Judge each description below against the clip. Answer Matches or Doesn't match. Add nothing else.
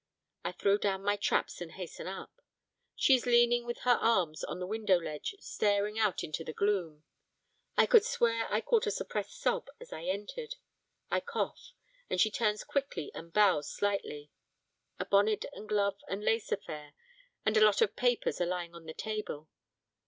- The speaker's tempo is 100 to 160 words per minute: Doesn't match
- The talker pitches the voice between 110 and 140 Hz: Doesn't match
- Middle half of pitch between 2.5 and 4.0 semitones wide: Doesn't match